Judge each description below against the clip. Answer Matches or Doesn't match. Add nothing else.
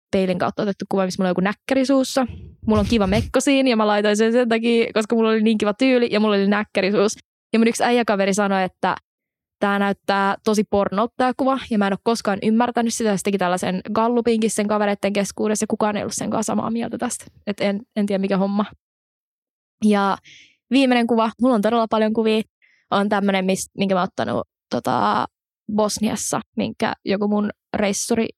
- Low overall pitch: Doesn't match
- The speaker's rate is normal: Doesn't match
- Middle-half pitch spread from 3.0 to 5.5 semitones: Doesn't match